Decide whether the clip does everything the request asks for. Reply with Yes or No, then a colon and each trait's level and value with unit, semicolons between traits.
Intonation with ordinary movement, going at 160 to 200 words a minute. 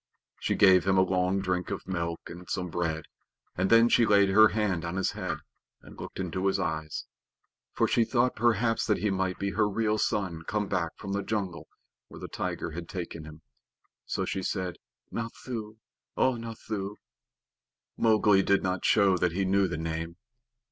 Yes: average, 3.3 semitones; average, 180 wpm